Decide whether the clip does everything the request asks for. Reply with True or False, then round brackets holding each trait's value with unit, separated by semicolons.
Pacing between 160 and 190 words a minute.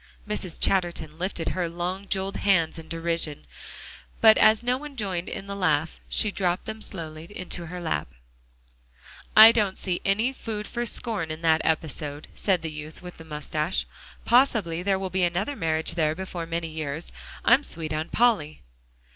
True (170 wpm)